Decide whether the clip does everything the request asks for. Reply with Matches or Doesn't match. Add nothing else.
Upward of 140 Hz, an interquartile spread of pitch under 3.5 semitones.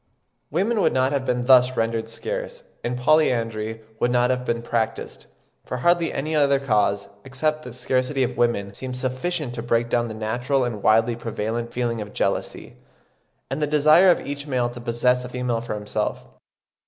Doesn't match